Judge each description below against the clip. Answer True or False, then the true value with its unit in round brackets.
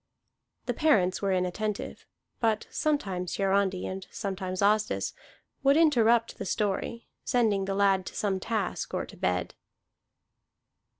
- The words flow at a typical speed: False (125 wpm)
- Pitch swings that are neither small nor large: True (3.2 semitones)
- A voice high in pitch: True (200 Hz)